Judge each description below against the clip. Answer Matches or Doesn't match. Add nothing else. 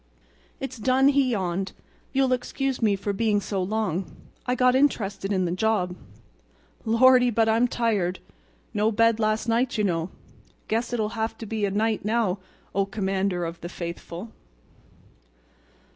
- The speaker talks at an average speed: Matches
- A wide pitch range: Doesn't match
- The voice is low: Doesn't match